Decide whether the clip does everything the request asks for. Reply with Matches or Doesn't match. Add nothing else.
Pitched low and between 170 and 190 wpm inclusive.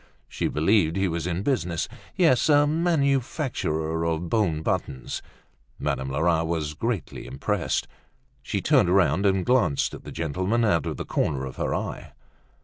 Doesn't match